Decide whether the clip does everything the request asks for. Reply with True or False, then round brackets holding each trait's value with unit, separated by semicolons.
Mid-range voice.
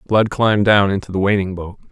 False (100 Hz)